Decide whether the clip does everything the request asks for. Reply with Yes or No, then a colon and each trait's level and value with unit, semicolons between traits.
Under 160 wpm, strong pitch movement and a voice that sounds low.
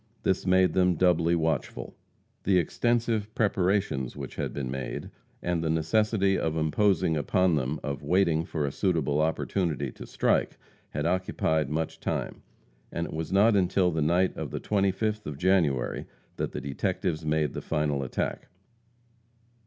No: average, 150 wpm; average, 3.8 semitones; very low, 85 Hz